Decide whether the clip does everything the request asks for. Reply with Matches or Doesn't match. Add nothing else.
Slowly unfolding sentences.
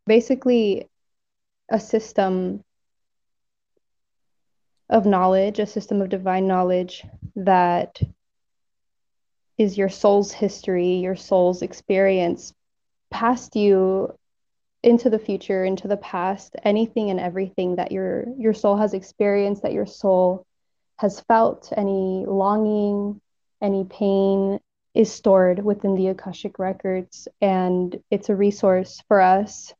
Matches